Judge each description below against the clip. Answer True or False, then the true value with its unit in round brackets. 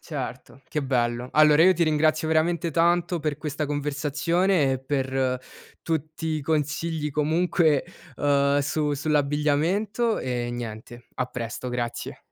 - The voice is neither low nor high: True (150 Hz)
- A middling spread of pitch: True (3.2 semitones)